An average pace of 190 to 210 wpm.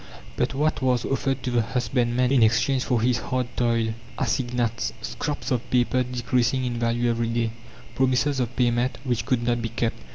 No: average, 175 wpm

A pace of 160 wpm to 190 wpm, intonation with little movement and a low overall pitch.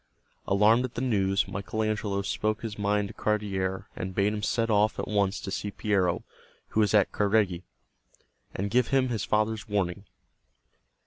Yes: average, 170 wpm; narrow, 1.7 semitones; low, 105 Hz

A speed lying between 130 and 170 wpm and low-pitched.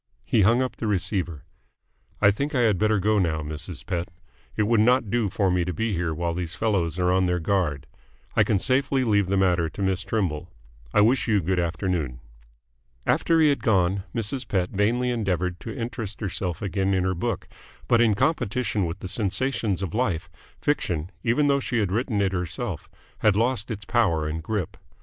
No: average, 195 wpm; low, 100 Hz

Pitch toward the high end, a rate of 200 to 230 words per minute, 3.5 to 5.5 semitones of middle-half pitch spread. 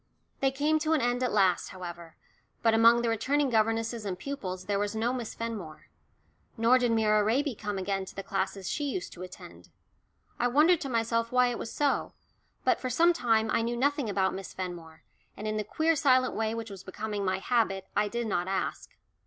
Yes: high, 225 Hz; fast, 205 wpm; average, 4.3 semitones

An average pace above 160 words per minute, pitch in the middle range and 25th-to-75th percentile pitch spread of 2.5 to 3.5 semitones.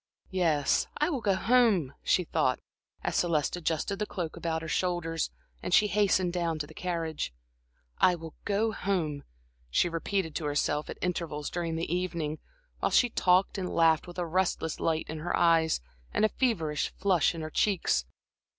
Yes: average, 175 wpm; medium, 170 Hz; average, 2.8 semitones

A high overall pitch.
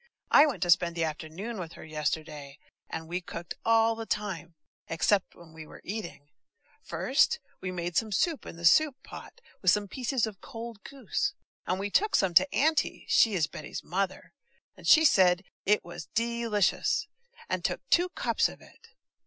Yes: high, 195 Hz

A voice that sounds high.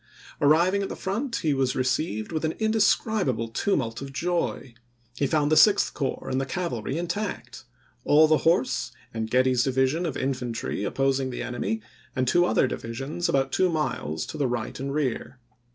No: low, 135 Hz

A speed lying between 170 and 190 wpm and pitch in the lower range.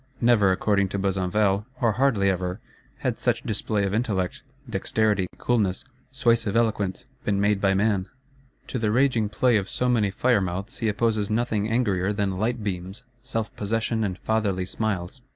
No: average, 160 wpm; low, 105 Hz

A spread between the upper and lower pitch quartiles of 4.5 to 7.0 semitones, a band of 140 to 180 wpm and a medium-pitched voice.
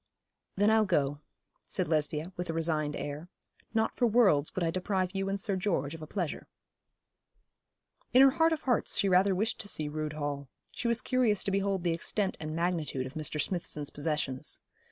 No: average, 5.0 semitones; average, 190 wpm; medium, 175 Hz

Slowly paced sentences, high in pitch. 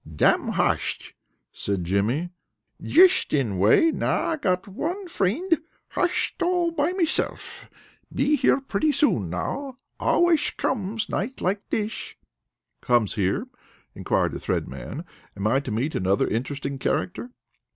Yes: slow, 130 wpm; high, 200 Hz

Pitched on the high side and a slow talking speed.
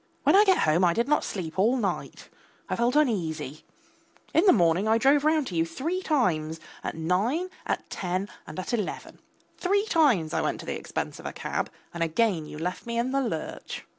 No: high, 220 Hz; fast, 205 wpm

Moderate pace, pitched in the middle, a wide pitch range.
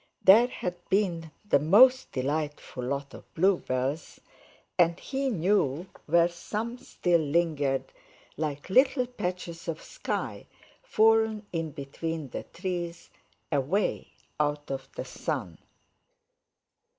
No: slow, 110 wpm; medium, 170 Hz; wide, 5.7 semitones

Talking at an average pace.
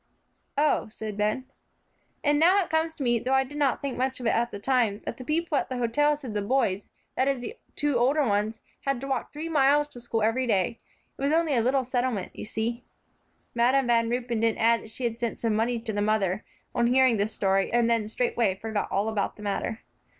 No: fast, 230 wpm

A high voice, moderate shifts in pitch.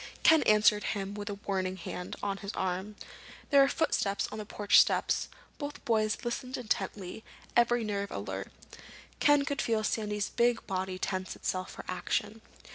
Yes: high, 210 Hz; average, 3.4 semitones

